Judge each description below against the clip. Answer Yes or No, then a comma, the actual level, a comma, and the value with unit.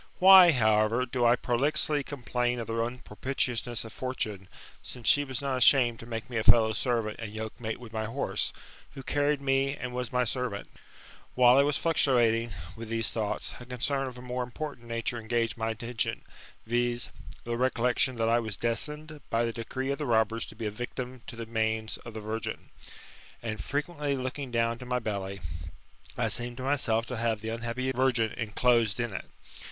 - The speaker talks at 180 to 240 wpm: Yes, average, 190 wpm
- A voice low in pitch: Yes, low, 120 Hz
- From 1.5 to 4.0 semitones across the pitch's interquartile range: Yes, narrow, 2.4 semitones